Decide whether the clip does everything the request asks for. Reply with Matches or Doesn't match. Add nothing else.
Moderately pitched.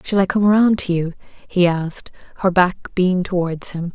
Matches